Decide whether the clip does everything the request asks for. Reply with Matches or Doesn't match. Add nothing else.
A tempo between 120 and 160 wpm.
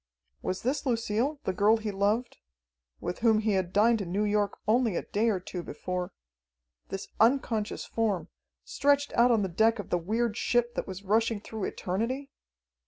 Doesn't match